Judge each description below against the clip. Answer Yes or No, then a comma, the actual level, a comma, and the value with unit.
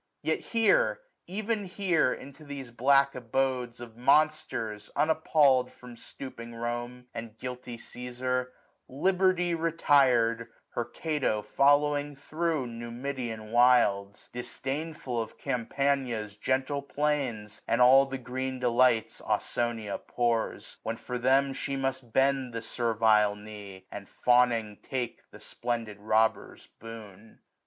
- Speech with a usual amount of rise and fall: Yes, average, 3.3 semitones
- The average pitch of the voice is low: Yes, low, 125 Hz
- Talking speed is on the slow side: Yes, slow, 120 wpm